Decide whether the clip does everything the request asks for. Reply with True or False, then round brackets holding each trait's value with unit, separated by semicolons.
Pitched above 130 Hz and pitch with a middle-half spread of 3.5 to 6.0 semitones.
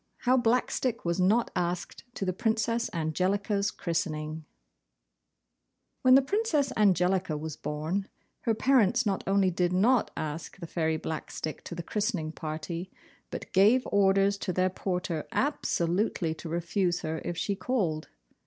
True (185 Hz; 4.6 semitones)